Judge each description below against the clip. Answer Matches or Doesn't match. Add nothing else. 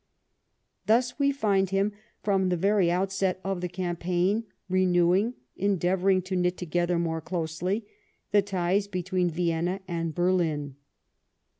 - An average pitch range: Doesn't match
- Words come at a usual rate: Doesn't match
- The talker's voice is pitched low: Doesn't match